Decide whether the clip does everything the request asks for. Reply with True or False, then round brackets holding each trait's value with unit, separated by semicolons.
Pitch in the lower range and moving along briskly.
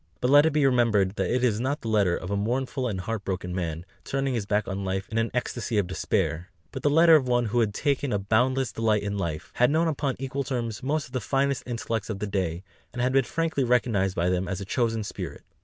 True (115 Hz; 250 wpm)